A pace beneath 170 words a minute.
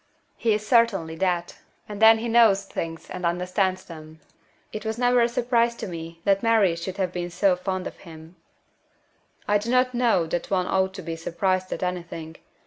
No: average, 190 wpm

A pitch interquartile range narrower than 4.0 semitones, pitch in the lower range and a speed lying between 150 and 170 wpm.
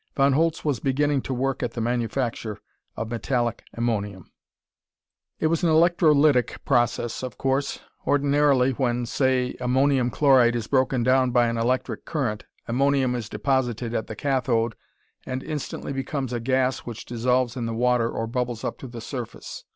Yes: narrow, 2.5 semitones; low, 125 Hz; average, 160 wpm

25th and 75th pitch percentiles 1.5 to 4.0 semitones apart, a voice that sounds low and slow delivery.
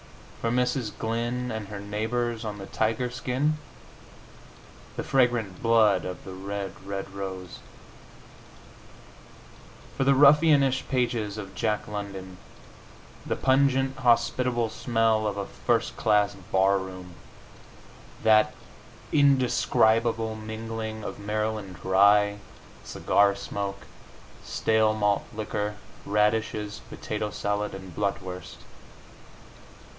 Yes: average, 2.9 semitones; low, 110 Hz; slow, 100 wpm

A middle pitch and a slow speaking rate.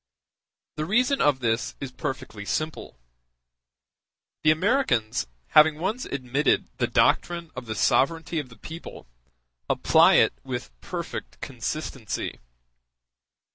Yes: medium, 150 Hz; slow, 110 wpm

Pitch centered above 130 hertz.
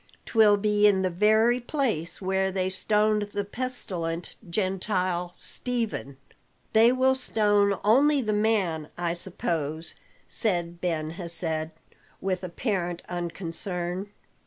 Yes: high, 190 Hz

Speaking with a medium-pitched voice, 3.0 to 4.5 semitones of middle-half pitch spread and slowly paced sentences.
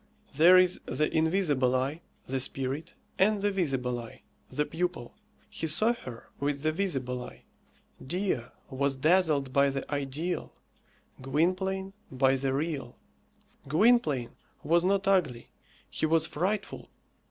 No: medium, 155 Hz; average, 5.3 semitones; slow, 130 wpm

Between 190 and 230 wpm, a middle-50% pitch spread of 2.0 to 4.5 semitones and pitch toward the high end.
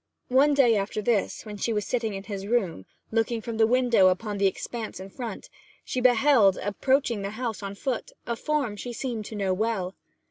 Yes: average, 200 wpm; average, 3.4 semitones; high, 220 Hz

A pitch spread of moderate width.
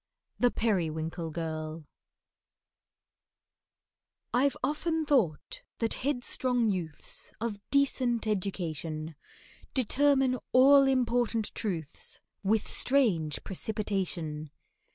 No: wide, 7.7 semitones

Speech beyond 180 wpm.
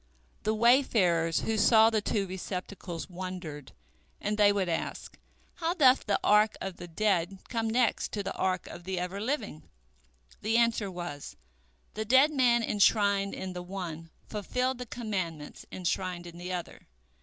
No: average, 155 wpm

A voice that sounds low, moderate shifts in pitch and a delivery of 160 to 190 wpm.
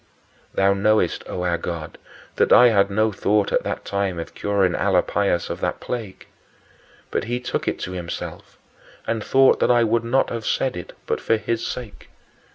Yes: low, 100 Hz; average, 3.9 semitones; average, 180 wpm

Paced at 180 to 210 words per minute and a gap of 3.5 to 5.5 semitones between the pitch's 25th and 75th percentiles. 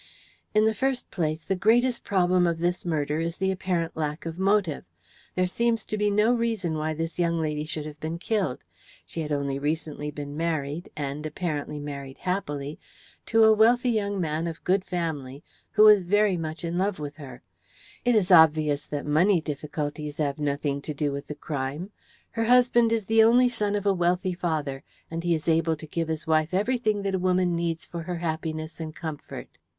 Yes: average, 195 wpm; average, 4.7 semitones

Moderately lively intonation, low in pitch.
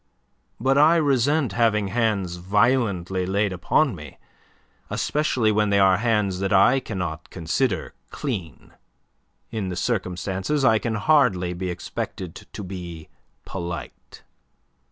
Yes: average, 4.9 semitones; low, 100 Hz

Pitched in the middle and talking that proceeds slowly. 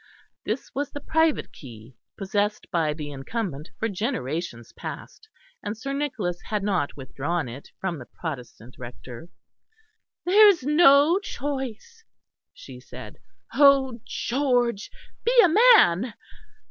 No: high, 215 Hz; slow, 120 wpm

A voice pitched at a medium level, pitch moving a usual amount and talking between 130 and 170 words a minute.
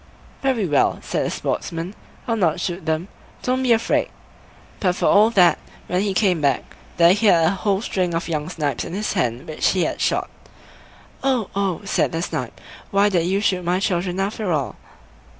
No: medium, 180 Hz; average, 3.4 semitones; average, 190 wpm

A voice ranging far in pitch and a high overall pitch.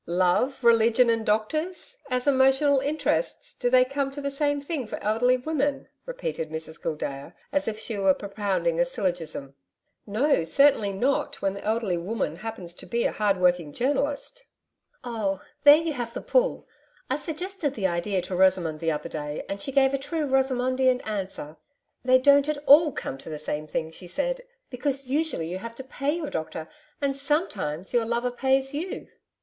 Yes: wide, 7.3 semitones; high, 245 Hz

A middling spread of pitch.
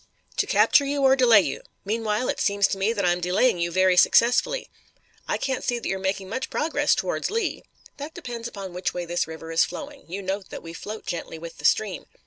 No: wide, 6.0 semitones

